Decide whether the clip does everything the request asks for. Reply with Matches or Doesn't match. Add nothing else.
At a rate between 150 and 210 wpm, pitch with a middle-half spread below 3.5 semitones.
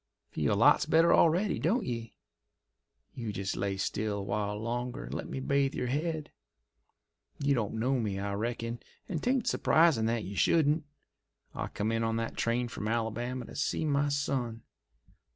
Doesn't match